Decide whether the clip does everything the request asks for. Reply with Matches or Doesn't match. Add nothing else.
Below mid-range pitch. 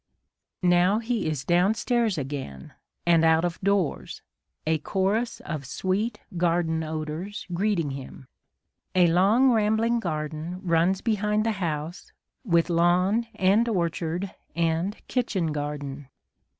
Doesn't match